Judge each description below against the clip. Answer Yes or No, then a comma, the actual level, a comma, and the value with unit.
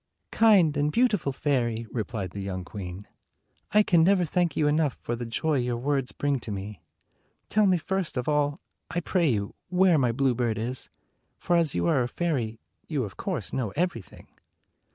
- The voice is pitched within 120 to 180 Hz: Yes, medium, 140 Hz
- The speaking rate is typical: Yes, average, 180 wpm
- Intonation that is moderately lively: No, wide, 6.6 semitones